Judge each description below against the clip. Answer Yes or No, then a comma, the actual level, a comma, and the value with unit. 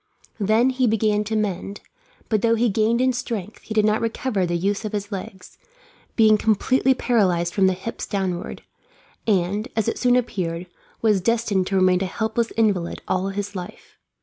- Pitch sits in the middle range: No, high, 210 Hz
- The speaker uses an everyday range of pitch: Yes, average, 3.1 semitones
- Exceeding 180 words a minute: No, average, 175 wpm